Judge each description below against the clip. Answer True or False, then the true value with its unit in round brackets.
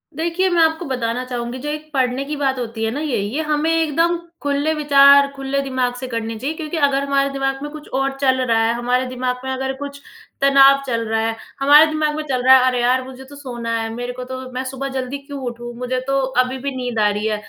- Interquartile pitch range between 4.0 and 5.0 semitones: False (2.4 semitones)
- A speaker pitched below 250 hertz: False (265 Hz)